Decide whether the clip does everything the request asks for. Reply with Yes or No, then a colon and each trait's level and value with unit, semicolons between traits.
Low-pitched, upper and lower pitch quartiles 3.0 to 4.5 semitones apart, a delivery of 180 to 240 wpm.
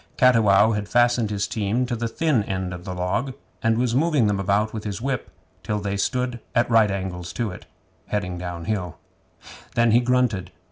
Yes: low, 110 Hz; average, 3.6 semitones; average, 185 wpm